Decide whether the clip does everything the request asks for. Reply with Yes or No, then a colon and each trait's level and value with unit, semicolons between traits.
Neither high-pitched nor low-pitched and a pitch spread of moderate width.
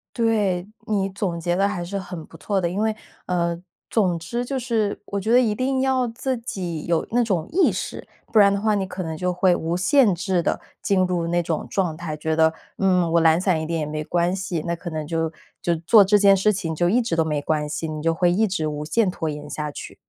Yes: medium, 180 Hz; average, 3.9 semitones